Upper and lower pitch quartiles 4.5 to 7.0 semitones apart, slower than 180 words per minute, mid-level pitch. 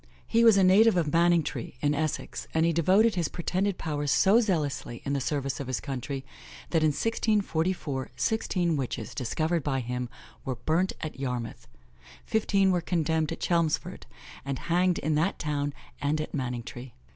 Yes: average, 4.8 semitones; average, 165 wpm; medium, 155 Hz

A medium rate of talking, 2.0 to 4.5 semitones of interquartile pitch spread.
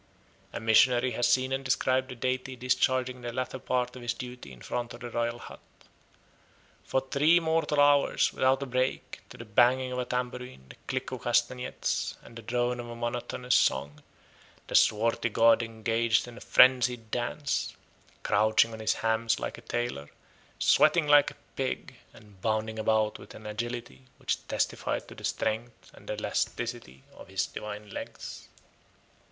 Yes: average, 165 wpm; narrow, 2.4 semitones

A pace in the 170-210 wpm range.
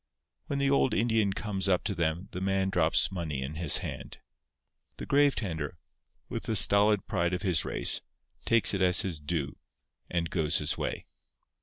Yes: average, 175 wpm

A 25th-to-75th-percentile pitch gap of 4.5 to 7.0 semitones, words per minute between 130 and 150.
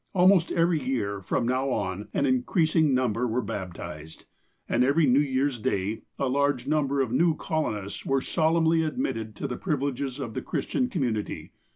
No: average, 5.1 semitones; average, 165 wpm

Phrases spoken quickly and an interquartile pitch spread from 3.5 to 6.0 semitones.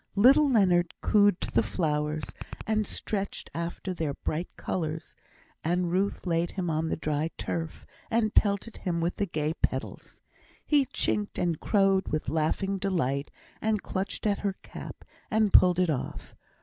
No: average, 155 wpm; average, 4.0 semitones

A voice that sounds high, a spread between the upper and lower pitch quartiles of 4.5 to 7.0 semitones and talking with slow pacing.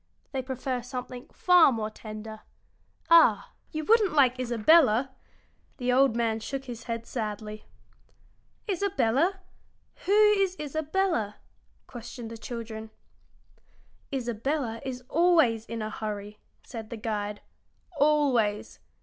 Yes: high, 245 Hz; average, 4.8 semitones; slow, 110 wpm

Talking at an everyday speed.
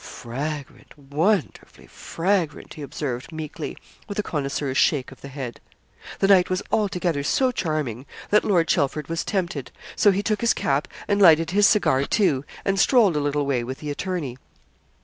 Yes: average, 170 wpm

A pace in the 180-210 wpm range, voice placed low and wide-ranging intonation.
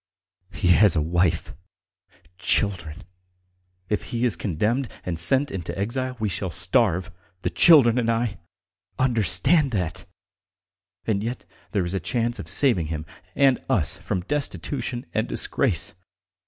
No: slow, 135 wpm; low, 105 Hz; wide, 6.0 semitones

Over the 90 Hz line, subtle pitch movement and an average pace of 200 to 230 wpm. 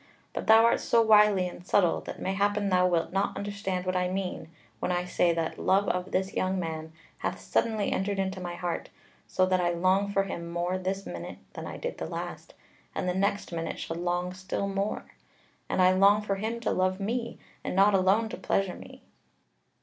Yes: high, 190 Hz; narrow, 2.0 semitones; fast, 205 wpm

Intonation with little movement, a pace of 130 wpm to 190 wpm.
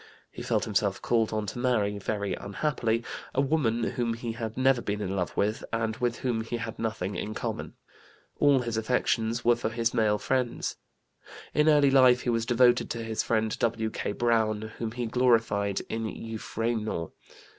Yes: narrow, 1.8 semitones; average, 175 wpm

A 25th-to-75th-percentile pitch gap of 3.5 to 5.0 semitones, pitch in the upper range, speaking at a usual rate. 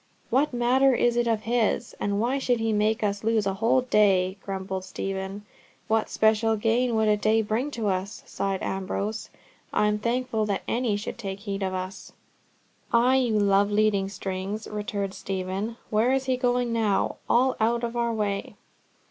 No: average, 3.1 semitones; high, 215 Hz; average, 175 wpm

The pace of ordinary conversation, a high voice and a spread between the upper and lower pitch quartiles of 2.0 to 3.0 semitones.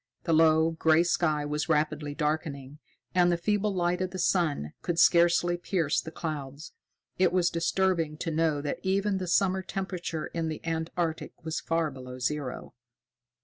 No: average, 160 wpm; medium, 165 Hz; narrow, 2.6 semitones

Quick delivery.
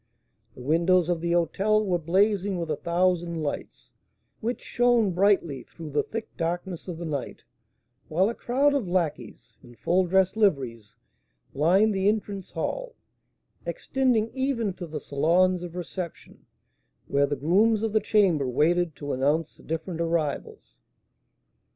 No: average, 145 wpm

